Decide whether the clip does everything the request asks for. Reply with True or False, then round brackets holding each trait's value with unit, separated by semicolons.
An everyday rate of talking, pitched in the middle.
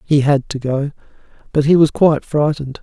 True (190 wpm; 145 Hz)